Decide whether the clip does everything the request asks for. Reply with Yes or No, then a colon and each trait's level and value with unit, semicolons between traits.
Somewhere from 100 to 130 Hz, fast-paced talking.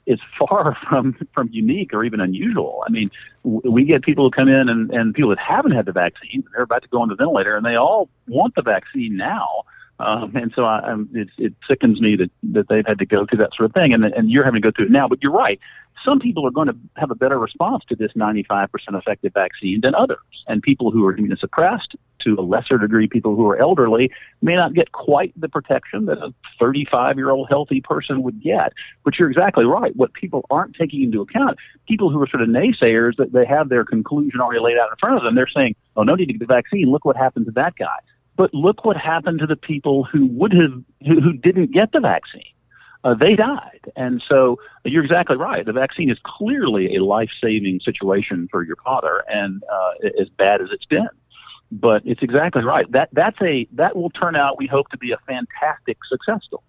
No: medium, 140 Hz; fast, 235 wpm